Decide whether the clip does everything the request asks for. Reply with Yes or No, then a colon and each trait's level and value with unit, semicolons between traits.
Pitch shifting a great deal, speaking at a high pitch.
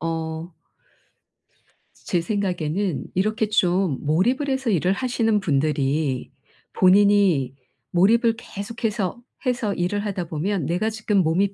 No: average, 4.7 semitones; high, 195 Hz